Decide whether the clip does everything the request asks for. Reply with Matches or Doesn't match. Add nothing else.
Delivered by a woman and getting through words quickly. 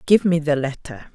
Matches